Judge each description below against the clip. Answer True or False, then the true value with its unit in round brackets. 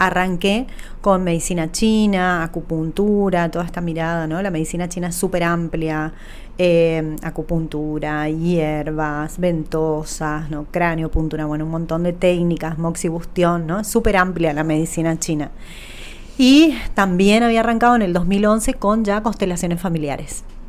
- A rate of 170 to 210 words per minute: False (130 wpm)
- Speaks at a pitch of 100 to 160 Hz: False (170 Hz)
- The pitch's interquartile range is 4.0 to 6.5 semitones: False (3.2 semitones)